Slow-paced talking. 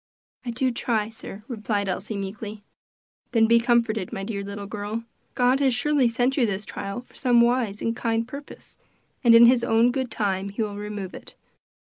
No: average, 190 wpm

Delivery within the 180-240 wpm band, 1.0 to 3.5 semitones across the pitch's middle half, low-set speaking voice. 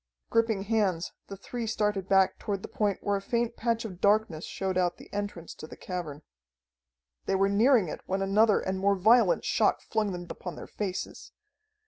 No: average, 185 wpm; average, 2.8 semitones; high, 200 Hz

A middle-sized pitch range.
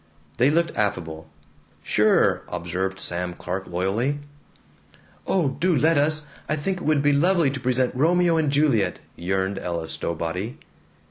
No: wide, 8.7 semitones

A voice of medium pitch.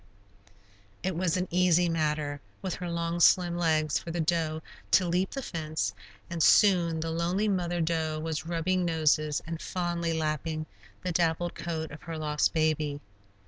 Yes: medium, 165 Hz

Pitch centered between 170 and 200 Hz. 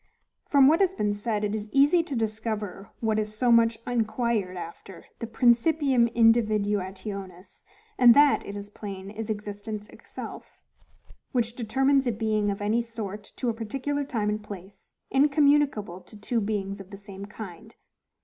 No: high, 220 Hz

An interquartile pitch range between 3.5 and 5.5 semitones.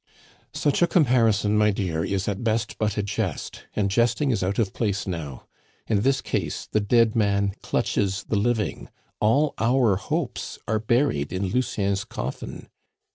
No: average, 3.0 semitones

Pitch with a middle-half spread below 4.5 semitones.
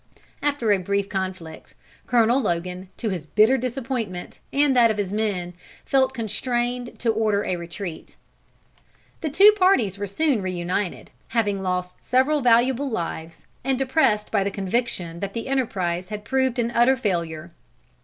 No: wide, 5.4 semitones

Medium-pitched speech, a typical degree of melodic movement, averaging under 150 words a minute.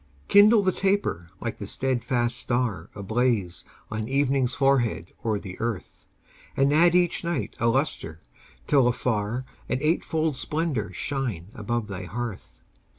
No: low, 125 Hz; average, 4.8 semitones; slow, 135 wpm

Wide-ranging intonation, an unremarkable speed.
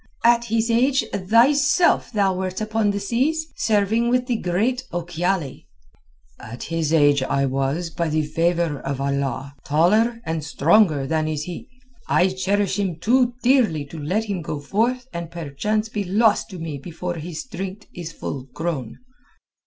Yes: wide, 6.0 semitones; average, 160 wpm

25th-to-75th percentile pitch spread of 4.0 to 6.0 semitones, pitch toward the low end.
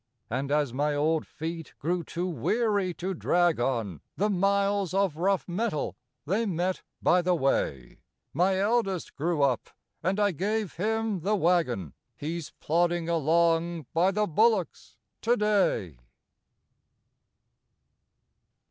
No: average, 4.3 semitones; medium, 175 Hz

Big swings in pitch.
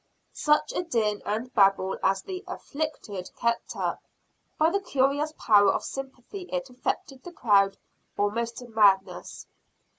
Yes: wide, 6.0 semitones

